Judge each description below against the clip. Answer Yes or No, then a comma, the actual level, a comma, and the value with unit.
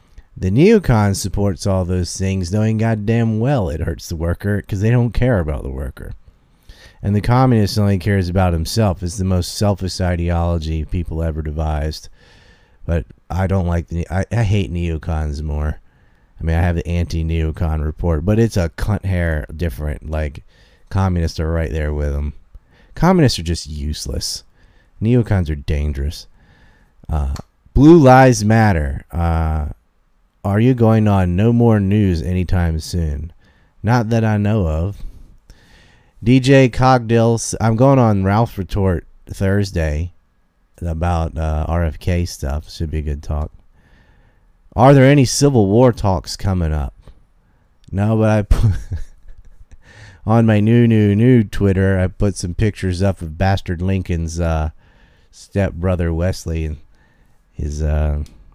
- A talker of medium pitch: No, very low, 90 Hz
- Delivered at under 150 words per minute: Yes, average, 140 wpm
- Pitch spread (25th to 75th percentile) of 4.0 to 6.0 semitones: Yes, average, 4.5 semitones